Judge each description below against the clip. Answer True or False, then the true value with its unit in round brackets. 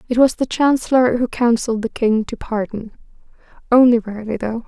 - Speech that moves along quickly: False (165 wpm)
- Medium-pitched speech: False (235 Hz)